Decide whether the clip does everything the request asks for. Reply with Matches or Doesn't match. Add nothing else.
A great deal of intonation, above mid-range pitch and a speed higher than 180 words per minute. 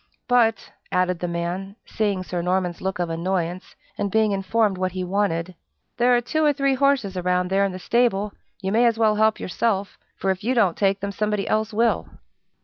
Doesn't match